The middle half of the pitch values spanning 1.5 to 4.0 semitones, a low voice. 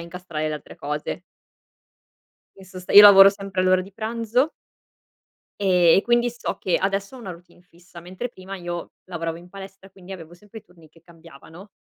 No: narrow, 2.4 semitones; medium, 185 Hz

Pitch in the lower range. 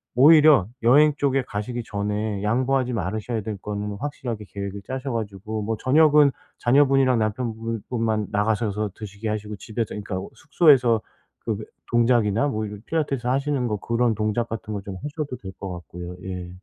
Yes: low, 110 Hz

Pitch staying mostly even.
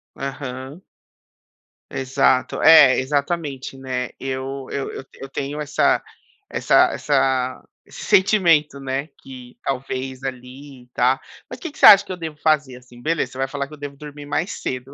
Yes: narrow, 2.3 semitones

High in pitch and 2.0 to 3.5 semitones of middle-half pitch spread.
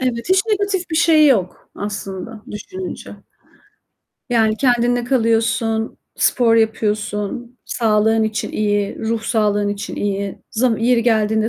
Yes: high, 225 Hz; average, 2.7 semitones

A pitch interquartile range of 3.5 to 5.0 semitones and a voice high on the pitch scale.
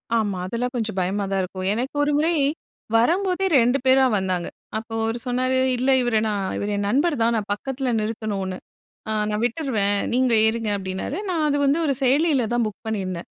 Yes: average, 4.6 semitones; high, 230 Hz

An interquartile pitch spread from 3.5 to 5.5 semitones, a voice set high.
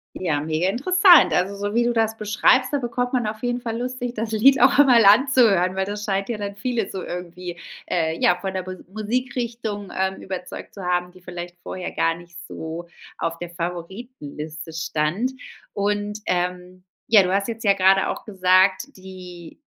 Yes: average, 4.4 semitones; high, 195 Hz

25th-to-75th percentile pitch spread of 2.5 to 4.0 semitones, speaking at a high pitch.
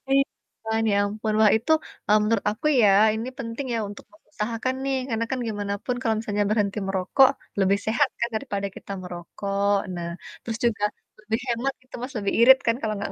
Yes: average, 2.9 semitones; high, 220 Hz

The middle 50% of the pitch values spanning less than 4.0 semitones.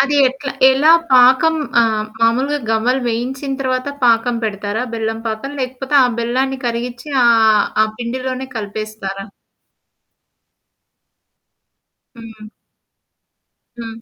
Yes: average, 2.8 semitones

